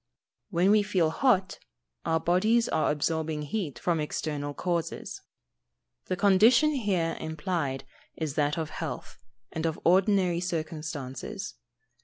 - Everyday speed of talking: No, slow, 125 wpm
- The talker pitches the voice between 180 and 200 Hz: No, medium, 170 Hz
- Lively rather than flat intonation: No, average, 3.8 semitones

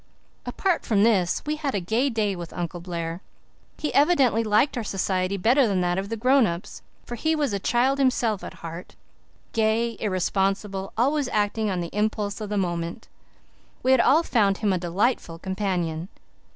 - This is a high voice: Yes, high, 210 Hz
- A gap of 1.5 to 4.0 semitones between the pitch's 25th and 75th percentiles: No, average, 4.7 semitones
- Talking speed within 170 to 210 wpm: Yes, average, 175 wpm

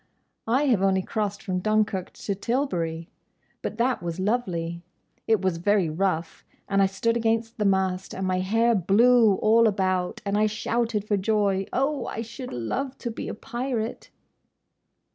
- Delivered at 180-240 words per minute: No, average, 160 wpm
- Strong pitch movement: No, average, 3.6 semitones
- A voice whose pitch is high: Yes, high, 205 Hz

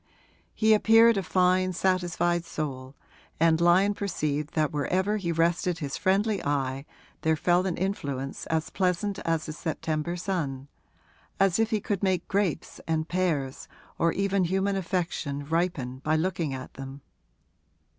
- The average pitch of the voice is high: No, medium, 170 Hz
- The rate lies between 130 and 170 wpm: Yes, average, 145 wpm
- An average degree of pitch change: Yes, average, 3.8 semitones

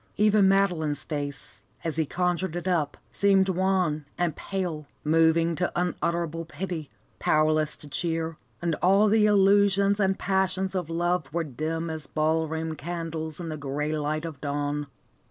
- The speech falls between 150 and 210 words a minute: Yes, average, 155 wpm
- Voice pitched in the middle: Yes, medium, 165 Hz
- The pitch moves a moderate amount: Yes, average, 3.4 semitones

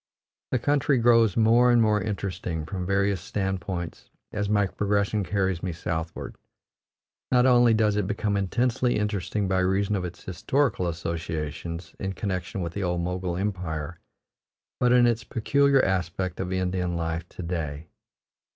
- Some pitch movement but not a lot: Yes, average, 3.7 semitones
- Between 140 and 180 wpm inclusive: Yes, average, 150 wpm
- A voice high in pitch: No, very low, 95 Hz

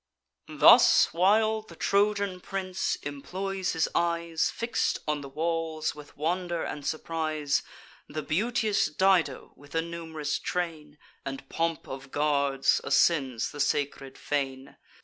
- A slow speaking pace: Yes, slow, 125 wpm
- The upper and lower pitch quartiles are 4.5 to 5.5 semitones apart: No, average, 3.9 semitones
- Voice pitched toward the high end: No, medium, 160 Hz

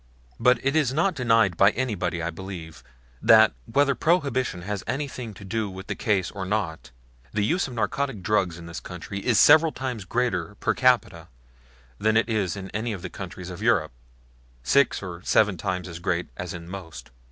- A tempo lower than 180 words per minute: No, average, 185 wpm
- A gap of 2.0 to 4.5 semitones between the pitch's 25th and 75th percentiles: No, wide, 5.5 semitones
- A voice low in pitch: Yes, low, 100 Hz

